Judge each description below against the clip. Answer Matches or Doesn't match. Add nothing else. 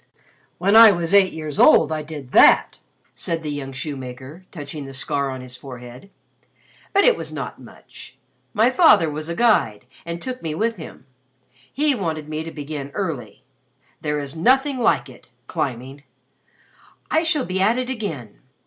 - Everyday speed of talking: Matches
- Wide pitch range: Matches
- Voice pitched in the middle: Matches